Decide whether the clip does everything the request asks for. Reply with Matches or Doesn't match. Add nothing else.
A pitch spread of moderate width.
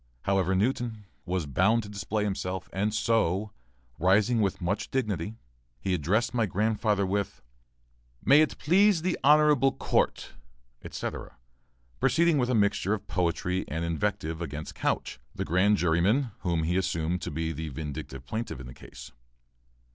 Matches